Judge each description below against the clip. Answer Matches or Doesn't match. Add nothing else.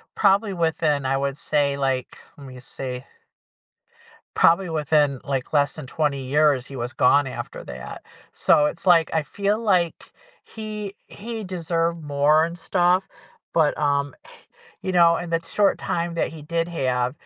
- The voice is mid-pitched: Matches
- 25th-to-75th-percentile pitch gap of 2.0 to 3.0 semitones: Doesn't match